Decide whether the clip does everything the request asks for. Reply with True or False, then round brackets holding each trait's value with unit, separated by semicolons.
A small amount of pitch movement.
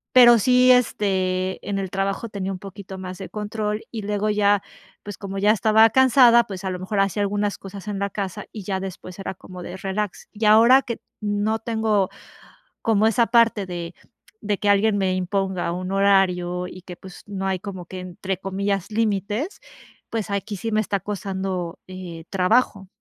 True (2.2 semitones)